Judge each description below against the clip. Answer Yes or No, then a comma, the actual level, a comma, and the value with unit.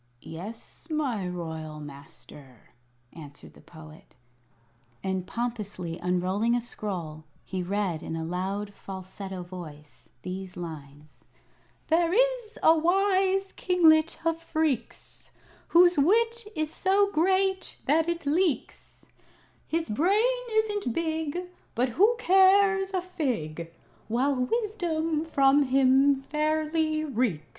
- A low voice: No, very high, 280 Hz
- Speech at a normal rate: No, slow, 110 wpm